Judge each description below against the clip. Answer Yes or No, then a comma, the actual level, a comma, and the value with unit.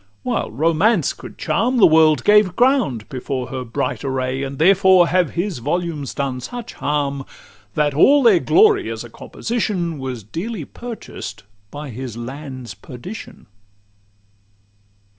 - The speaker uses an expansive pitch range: Yes, wide, 7.2 semitones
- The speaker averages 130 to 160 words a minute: Yes, slow, 135 wpm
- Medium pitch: Yes, medium, 155 Hz